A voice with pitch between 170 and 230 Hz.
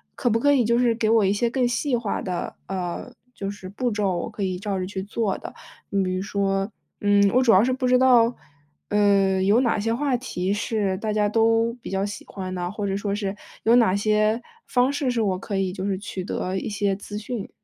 Yes: high, 205 Hz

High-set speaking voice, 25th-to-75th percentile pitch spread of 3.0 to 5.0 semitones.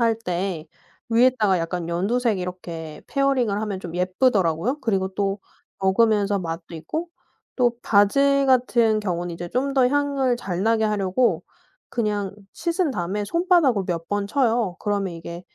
No: high, 205 Hz; wide, 5.5 semitones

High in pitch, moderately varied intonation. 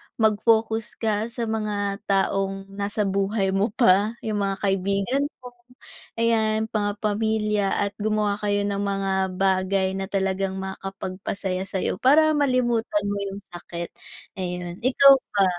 No: high, 205 Hz; narrow, 2.2 semitones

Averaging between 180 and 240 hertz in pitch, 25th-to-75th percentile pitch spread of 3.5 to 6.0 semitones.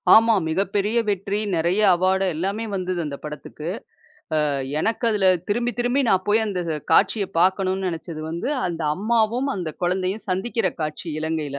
Yes: high, 190 Hz; average, 4.2 semitones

